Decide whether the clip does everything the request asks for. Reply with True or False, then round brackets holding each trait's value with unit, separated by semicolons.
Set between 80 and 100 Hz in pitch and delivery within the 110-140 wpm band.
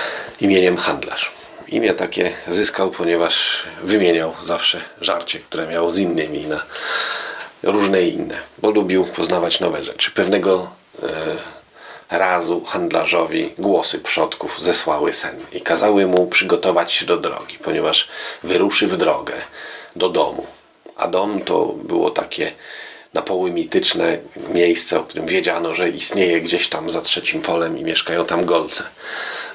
True (95 Hz; 130 wpm)